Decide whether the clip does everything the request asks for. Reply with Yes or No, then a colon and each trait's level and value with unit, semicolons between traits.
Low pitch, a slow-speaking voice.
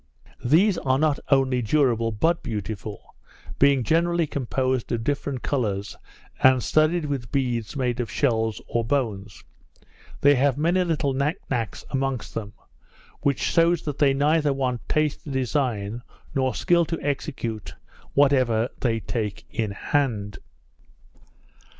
Yes: low, 130 Hz; slow, 130 wpm